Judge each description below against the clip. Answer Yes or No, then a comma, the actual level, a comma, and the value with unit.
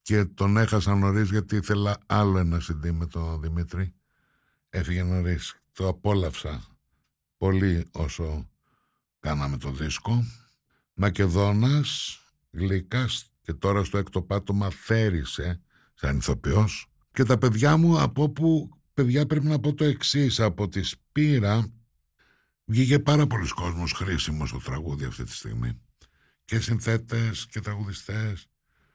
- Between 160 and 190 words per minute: No, average, 125 wpm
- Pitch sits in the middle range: No, low, 100 Hz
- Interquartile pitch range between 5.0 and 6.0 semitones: Yes, average, 5.3 semitones